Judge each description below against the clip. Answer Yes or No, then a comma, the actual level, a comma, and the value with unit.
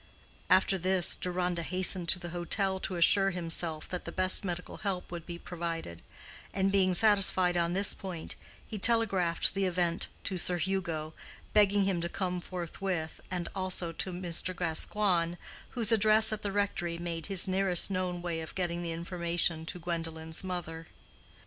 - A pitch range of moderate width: No, narrow, 2.1 semitones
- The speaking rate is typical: Yes, average, 160 wpm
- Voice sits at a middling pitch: Yes, medium, 180 Hz